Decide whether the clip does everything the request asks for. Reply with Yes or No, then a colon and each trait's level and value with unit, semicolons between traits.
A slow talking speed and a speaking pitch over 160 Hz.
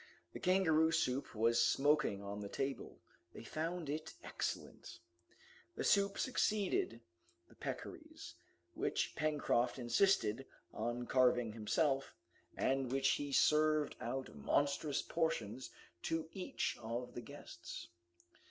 No: slow, 120 wpm; low, 135 Hz